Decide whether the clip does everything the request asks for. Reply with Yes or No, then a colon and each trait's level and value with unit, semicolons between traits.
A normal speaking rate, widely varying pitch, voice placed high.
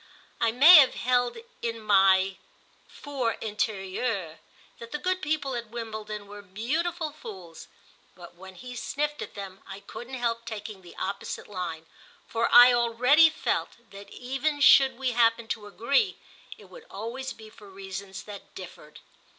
No: average, 150 wpm; average, 4.6 semitones; high, 230 Hz